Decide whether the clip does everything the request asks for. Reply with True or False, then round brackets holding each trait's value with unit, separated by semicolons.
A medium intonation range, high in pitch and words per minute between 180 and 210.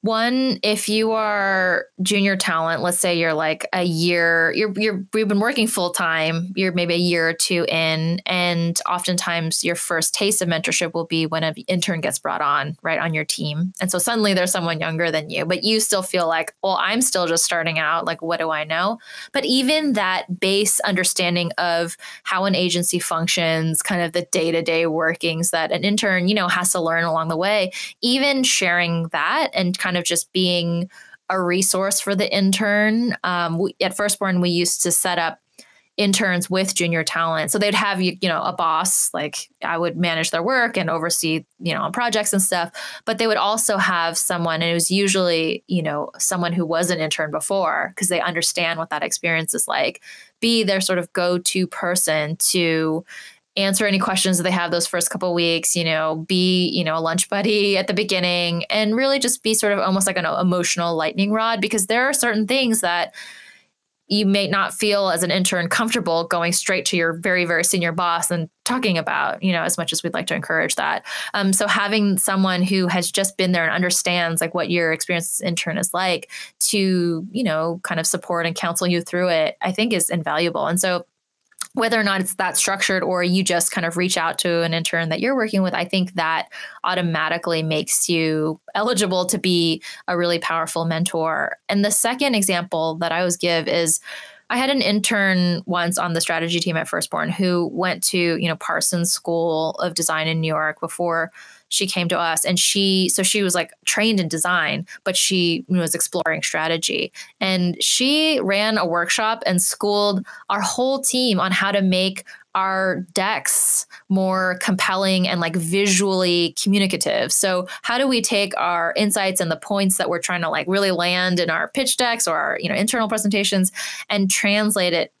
False (3.0 semitones; 180 Hz; 200 wpm)